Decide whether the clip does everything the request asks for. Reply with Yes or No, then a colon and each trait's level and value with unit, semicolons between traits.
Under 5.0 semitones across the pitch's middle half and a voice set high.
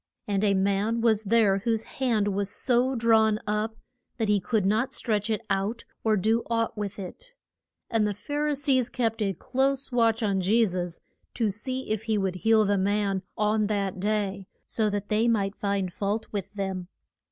Yes: narrow, 2.4 semitones; high, 210 Hz